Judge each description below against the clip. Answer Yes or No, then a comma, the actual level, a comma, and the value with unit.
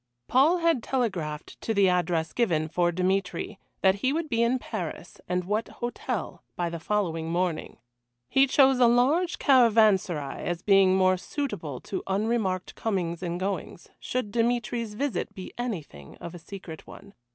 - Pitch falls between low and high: No, high, 195 Hz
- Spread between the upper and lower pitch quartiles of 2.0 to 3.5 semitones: No, wide, 5.4 semitones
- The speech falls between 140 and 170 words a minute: Yes, average, 160 wpm